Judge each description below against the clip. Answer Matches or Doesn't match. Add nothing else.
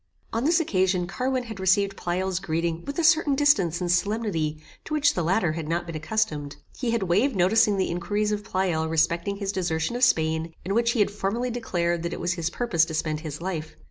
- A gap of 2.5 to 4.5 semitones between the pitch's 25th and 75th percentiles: Doesn't match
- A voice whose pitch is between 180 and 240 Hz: Matches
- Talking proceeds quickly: Matches